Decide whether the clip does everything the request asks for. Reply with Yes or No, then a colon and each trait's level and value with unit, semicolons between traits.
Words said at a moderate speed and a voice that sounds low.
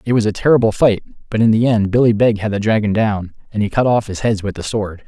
No: fast, 285 wpm; low, 110 Hz